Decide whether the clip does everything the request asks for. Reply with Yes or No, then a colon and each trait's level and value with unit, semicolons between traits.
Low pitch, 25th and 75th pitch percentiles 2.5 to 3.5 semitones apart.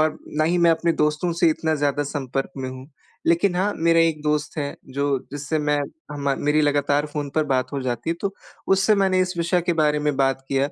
No: medium, 150 Hz; average, 2.9 semitones